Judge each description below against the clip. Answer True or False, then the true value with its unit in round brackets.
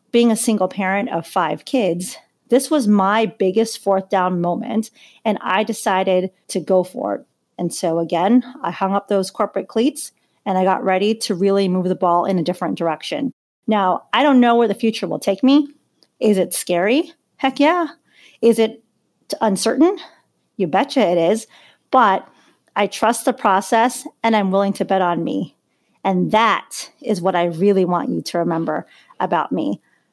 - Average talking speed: True (175 wpm)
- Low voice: False (205 Hz)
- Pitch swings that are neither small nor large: True (3.9 semitones)